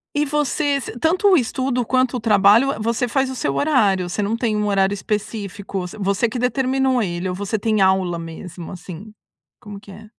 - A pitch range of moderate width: Yes, average, 4.9 semitones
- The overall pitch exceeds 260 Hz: No, high, 215 Hz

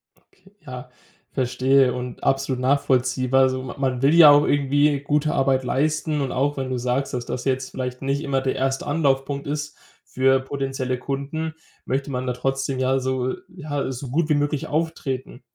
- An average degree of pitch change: No, narrow, 1.9 semitones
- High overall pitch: No, low, 135 Hz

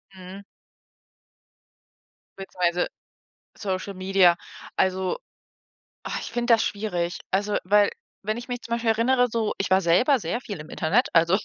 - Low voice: No, high, 195 Hz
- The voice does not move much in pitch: No, average, 3.9 semitones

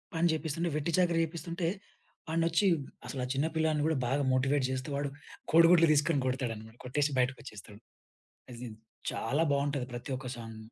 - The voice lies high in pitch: No, medium, 145 Hz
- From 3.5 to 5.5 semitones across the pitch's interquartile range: Yes, average, 4.2 semitones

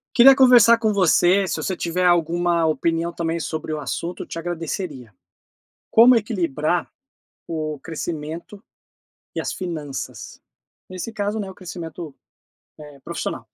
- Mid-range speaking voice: Yes, medium, 170 Hz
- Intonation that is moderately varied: Yes, average, 3.5 semitones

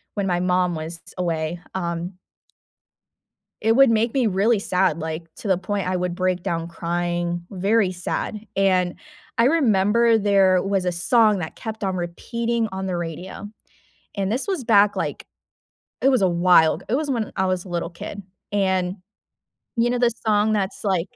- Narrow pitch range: No, average, 3.7 semitones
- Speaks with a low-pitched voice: No, high, 190 Hz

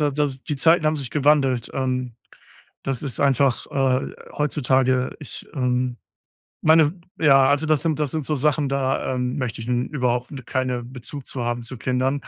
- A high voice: No, low, 135 Hz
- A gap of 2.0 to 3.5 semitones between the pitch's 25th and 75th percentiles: Yes, narrow, 2.6 semitones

